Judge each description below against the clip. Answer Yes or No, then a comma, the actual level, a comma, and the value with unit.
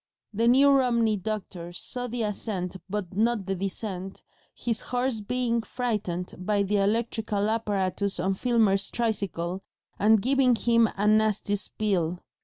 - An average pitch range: Yes, average, 3.2 semitones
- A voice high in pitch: Yes, high, 210 Hz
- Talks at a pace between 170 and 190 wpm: No, slow, 135 wpm